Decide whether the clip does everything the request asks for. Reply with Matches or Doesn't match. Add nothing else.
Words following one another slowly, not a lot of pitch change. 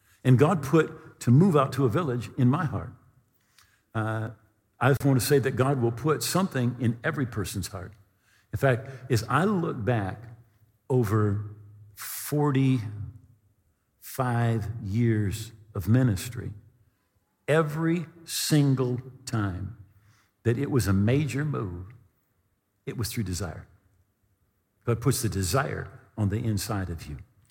Doesn't match